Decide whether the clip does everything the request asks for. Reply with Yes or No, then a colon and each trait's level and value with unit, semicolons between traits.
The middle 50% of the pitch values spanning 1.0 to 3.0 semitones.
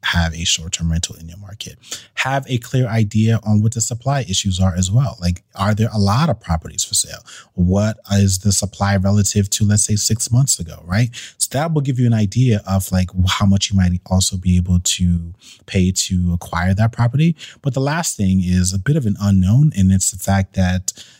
No: average, 3.7 semitones